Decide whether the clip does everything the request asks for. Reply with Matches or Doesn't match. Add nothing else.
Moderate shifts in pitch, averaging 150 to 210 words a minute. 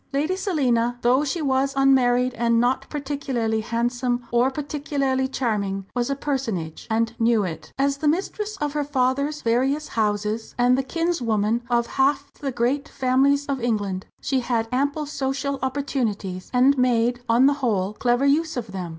Matches